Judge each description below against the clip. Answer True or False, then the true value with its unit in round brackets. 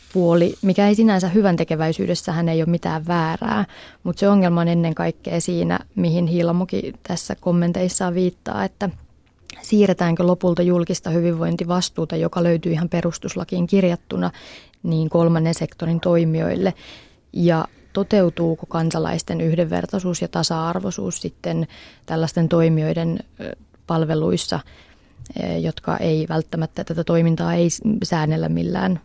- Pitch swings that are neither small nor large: False (1.6 semitones)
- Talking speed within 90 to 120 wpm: True (110 wpm)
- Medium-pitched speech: True (170 Hz)